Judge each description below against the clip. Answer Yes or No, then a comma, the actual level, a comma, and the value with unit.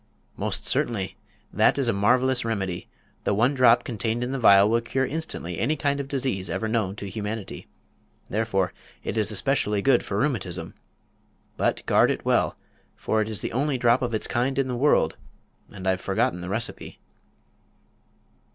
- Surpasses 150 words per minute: Yes, average, 170 wpm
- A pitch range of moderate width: Yes, average, 4.6 semitones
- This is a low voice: Yes, low, 115 Hz